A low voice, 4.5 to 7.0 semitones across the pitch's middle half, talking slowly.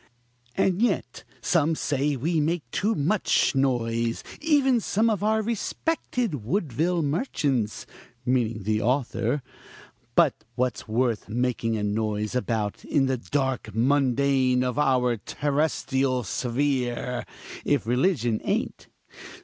Yes: low, 130 Hz; average, 5.1 semitones; slow, 115 wpm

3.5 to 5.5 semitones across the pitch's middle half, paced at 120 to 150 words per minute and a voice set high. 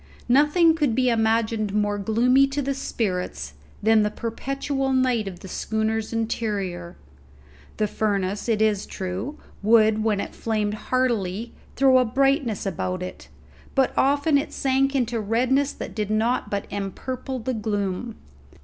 Yes: average, 3.9 semitones; average, 140 wpm; high, 225 Hz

